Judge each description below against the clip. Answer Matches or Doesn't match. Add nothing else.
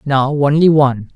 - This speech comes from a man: Matches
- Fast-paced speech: Doesn't match